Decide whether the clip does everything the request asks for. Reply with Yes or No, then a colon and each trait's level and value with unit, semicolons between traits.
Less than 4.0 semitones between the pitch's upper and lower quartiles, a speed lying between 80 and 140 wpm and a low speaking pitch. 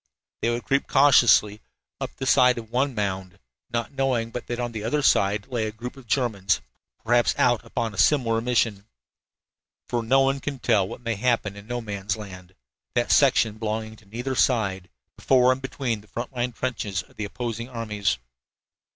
No: average, 3.0 semitones; average, 185 wpm; low, 115 Hz